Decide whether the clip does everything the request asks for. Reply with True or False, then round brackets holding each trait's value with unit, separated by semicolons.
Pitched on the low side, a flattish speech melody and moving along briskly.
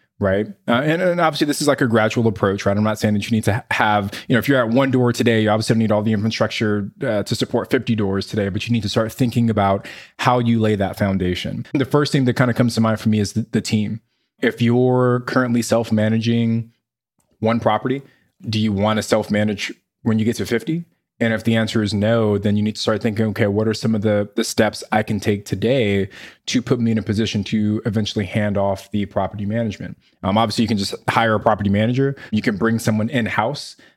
True (110 Hz; 2.1 semitones; 245 wpm)